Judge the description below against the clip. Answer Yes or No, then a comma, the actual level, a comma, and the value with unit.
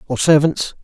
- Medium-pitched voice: Yes, medium, 145 Hz